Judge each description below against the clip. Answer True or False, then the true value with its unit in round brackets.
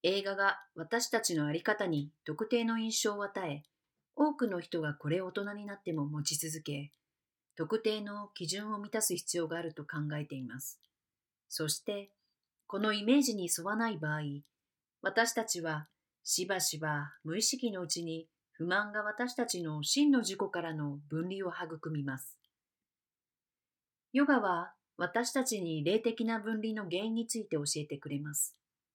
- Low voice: False (180 Hz)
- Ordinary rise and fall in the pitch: False (5.8 semitones)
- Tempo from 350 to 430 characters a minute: False (285 characters per minute)